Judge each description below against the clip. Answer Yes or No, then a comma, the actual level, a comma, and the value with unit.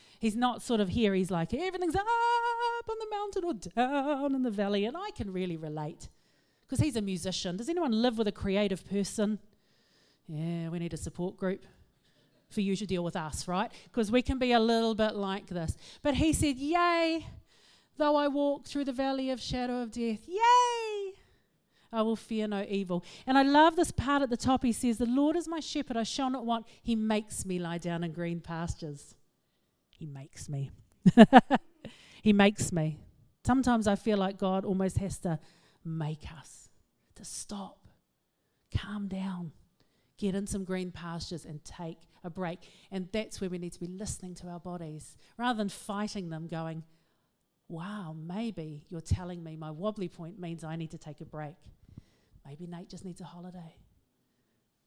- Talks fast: No, average, 185 wpm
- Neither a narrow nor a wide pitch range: No, wide, 6.4 semitones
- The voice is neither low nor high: No, high, 200 Hz